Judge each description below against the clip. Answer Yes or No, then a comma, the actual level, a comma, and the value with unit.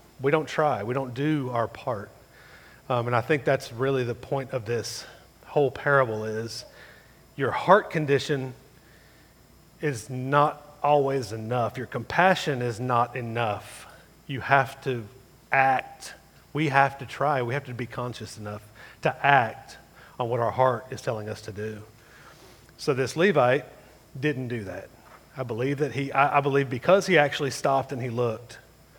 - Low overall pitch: Yes, low, 130 Hz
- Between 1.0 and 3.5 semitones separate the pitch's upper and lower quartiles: Yes, average, 2.9 semitones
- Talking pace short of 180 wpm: Yes, average, 160 wpm